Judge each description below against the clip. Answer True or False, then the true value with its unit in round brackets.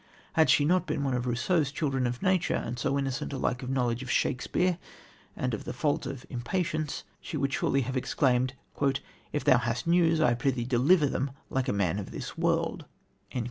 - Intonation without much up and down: False (3.7 semitones)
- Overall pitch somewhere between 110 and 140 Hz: True (135 Hz)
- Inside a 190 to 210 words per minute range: True (195 wpm)